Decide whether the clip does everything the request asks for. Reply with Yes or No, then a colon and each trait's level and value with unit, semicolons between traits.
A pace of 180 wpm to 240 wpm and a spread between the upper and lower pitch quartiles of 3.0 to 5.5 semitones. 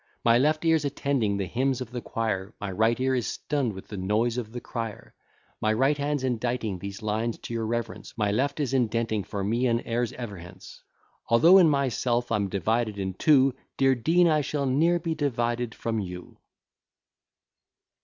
Yes: average, 185 wpm; average, 3.9 semitones